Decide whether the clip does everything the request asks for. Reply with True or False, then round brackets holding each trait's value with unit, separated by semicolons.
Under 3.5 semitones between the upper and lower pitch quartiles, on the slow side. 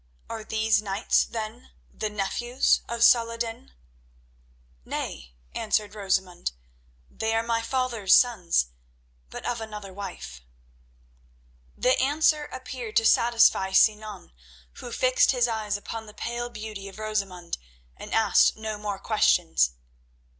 True (2.9 semitones; 125 wpm)